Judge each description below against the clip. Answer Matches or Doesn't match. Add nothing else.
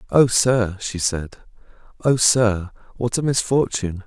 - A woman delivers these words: Doesn't match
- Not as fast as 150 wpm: Matches